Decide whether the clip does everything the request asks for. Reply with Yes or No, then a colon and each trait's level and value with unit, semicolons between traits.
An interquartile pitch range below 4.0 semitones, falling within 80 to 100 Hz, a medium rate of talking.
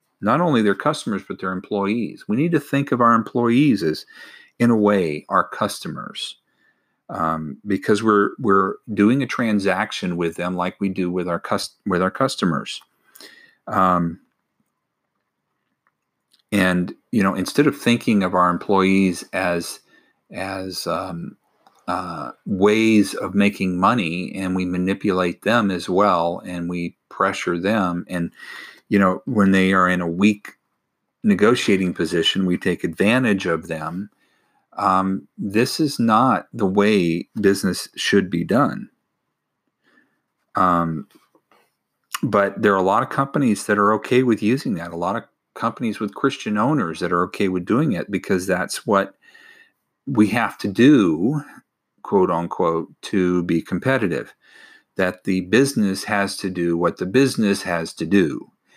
Yes: average, 3.2 semitones; very low, 95 Hz; average, 145 wpm